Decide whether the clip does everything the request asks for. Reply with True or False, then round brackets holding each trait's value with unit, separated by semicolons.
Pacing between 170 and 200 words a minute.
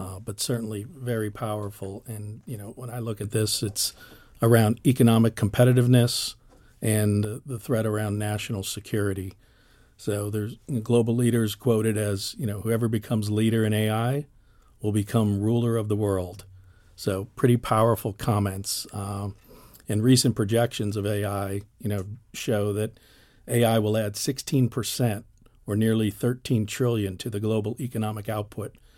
False (150 wpm)